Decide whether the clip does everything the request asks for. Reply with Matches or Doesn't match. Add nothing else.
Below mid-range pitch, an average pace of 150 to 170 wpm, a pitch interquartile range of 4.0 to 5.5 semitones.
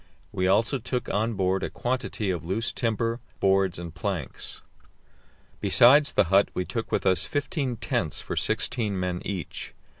Matches